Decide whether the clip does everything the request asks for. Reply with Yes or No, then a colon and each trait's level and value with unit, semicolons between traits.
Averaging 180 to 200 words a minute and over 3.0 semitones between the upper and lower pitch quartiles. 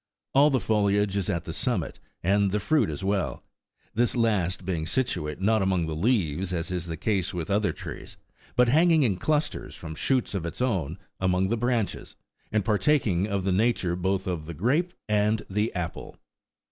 Yes: average, 185 wpm; average, 4.6 semitones